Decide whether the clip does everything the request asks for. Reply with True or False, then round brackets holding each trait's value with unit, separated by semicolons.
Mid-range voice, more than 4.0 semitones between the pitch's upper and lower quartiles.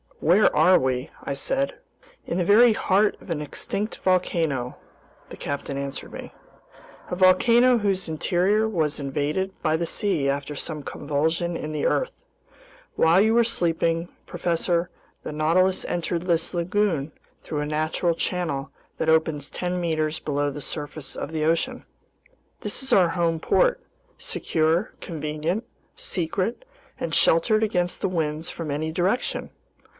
False (170 Hz; 3.5 semitones)